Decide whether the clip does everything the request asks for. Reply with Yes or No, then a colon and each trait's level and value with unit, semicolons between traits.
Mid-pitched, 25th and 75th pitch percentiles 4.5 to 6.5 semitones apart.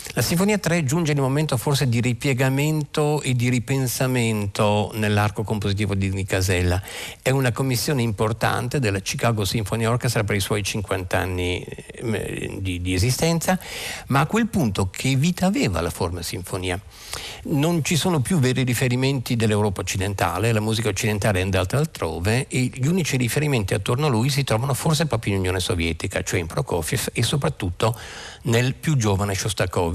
No: low, 115 Hz; wide, 5.4 semitones